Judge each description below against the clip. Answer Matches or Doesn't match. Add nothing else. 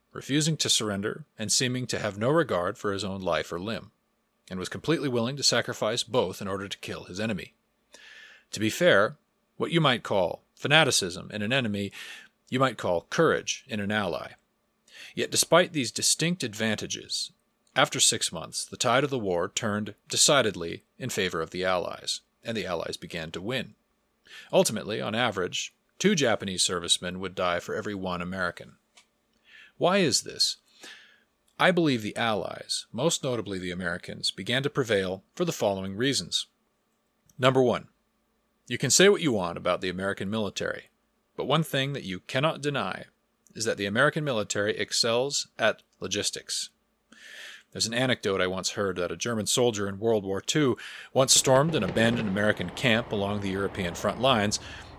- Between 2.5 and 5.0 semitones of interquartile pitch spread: Doesn't match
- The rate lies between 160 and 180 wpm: Matches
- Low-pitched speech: Matches